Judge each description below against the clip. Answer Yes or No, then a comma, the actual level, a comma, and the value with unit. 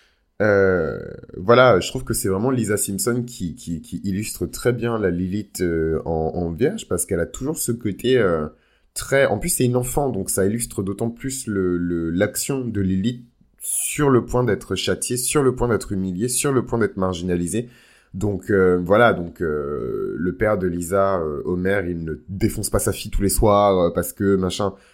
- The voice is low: Yes, low, 100 Hz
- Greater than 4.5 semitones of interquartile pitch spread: Yes, average, 4.9 semitones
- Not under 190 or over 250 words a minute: Yes, average, 195 wpm